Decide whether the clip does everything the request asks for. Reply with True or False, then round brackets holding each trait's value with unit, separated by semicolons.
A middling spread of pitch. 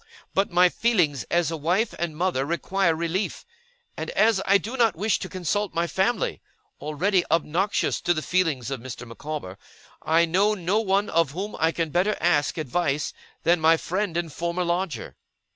True (3.4 semitones)